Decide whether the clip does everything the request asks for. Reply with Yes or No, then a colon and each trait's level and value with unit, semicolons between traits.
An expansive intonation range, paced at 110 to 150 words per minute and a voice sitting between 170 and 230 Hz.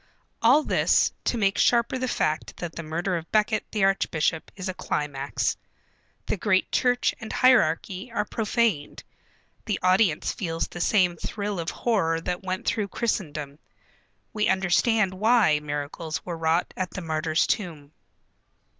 No: average, 4.8 semitones; average, 145 wpm; medium, 185 Hz